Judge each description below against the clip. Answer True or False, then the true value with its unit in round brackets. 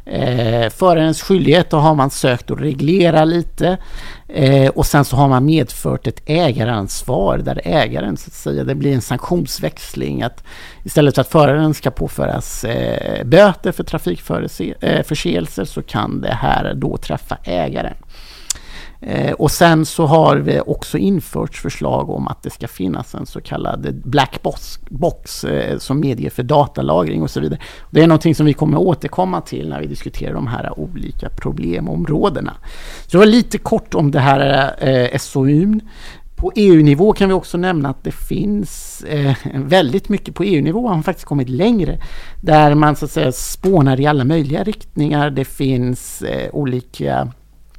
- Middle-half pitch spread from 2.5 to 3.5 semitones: False (4.3 semitones)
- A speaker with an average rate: True (165 wpm)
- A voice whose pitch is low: False (150 Hz)